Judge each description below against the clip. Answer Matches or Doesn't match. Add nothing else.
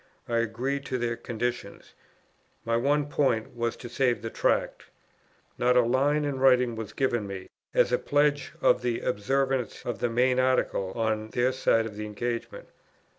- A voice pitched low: Matches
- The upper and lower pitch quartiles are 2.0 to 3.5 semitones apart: Matches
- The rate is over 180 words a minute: Doesn't match